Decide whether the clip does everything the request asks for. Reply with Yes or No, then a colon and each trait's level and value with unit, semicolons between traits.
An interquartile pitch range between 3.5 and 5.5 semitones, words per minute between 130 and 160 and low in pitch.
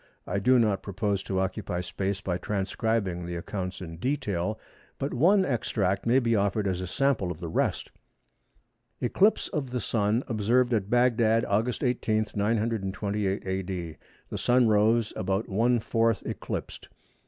Yes: average, 3.8 semitones; average, 145 wpm; low, 105 Hz